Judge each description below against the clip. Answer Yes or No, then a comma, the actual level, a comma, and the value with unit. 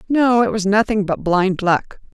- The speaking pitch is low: No, high, 205 Hz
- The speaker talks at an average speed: Yes, average, 190 wpm